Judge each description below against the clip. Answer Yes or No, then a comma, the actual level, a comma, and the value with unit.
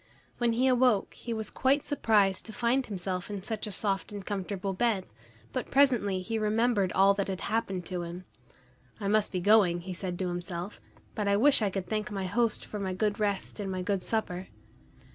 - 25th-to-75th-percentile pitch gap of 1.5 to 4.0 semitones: Yes, average, 3.0 semitones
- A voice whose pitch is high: Yes, high, 200 Hz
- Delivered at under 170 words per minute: No, average, 200 wpm